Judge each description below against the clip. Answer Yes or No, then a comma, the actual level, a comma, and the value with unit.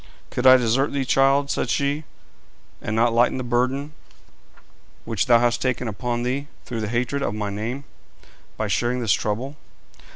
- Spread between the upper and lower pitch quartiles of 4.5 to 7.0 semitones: No, average, 2.7 semitones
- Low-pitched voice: Yes, low, 125 Hz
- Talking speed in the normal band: Yes, average, 165 wpm